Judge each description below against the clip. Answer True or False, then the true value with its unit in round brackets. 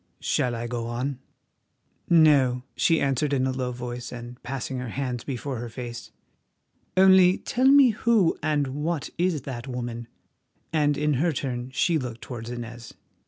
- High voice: False (130 Hz)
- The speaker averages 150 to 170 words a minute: True (160 wpm)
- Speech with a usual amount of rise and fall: True (3.9 semitones)